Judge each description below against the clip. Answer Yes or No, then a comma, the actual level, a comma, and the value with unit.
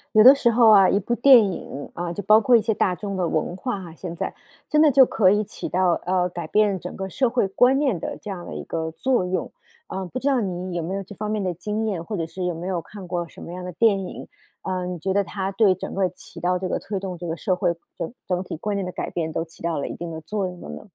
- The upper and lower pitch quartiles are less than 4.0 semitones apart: Yes, average, 3.2 semitones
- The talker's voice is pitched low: No, high, 190 Hz